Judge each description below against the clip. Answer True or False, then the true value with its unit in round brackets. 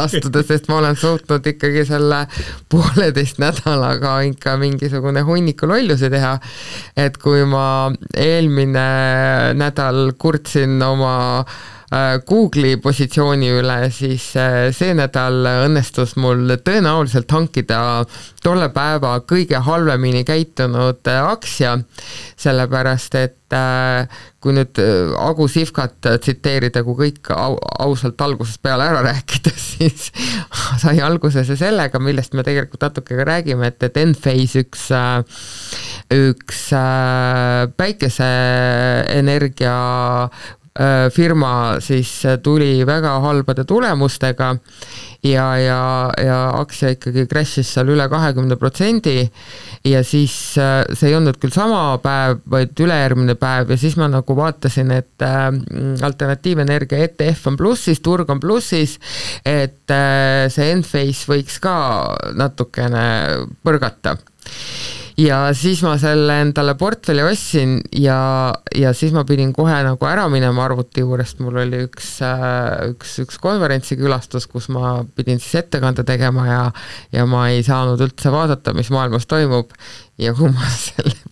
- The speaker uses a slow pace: True (115 wpm)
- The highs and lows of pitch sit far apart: False (2.6 semitones)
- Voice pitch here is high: False (135 Hz)